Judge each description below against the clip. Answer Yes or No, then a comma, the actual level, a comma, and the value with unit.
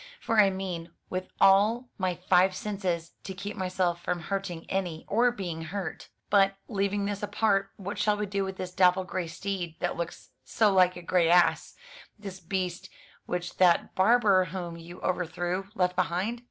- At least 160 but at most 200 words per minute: Yes, average, 170 wpm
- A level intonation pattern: Yes, narrow, 2.0 semitones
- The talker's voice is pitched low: No, medium, 185 Hz